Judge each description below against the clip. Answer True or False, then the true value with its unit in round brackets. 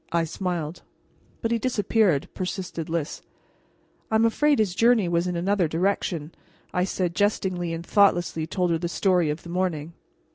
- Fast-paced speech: False (155 wpm)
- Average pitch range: True (3.2 semitones)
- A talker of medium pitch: True (180 Hz)